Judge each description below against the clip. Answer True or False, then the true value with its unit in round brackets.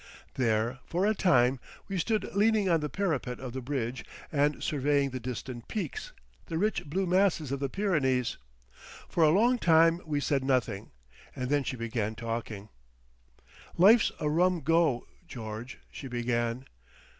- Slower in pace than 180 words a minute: True (155 wpm)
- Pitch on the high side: False (140 Hz)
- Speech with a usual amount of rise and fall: False (6.2 semitones)